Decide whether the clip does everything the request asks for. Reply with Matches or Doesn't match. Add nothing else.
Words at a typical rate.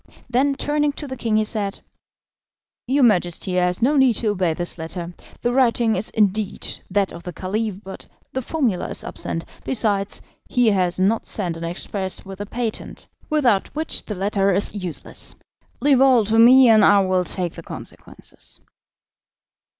Matches